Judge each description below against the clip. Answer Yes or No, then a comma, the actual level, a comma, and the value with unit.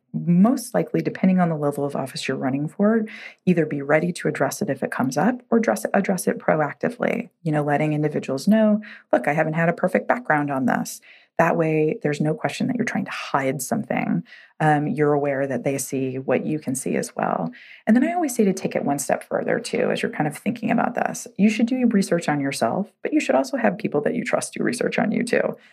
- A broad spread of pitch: Yes, wide, 7.3 semitones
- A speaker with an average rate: No, fast, 245 wpm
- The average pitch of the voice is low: No, medium, 170 Hz